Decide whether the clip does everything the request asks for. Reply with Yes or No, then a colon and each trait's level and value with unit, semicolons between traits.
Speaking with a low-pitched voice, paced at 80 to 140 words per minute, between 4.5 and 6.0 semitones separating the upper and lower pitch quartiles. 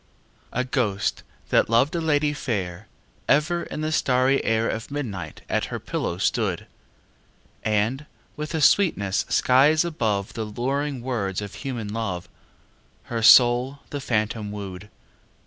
Yes: low, 120 Hz; slow, 135 wpm; wide, 5.5 semitones